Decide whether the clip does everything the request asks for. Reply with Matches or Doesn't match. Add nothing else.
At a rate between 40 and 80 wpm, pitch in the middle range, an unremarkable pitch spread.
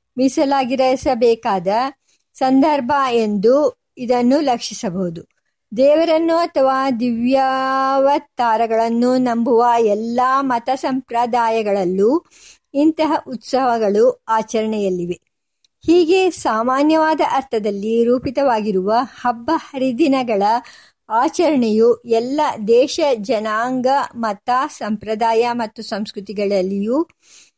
Doesn't match